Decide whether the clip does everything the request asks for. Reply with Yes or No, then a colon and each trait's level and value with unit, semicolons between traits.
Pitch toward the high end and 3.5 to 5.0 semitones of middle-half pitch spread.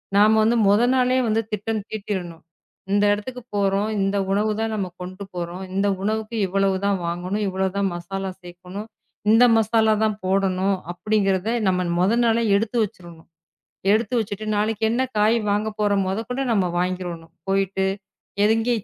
No: high, 200 Hz; average, 2.7 semitones